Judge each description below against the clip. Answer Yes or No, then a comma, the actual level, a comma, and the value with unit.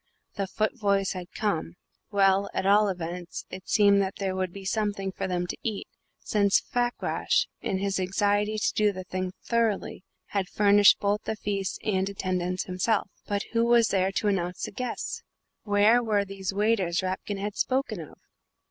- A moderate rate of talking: Yes, average, 170 wpm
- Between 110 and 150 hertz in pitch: No, high, 200 Hz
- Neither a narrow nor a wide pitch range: No, narrow, 2.0 semitones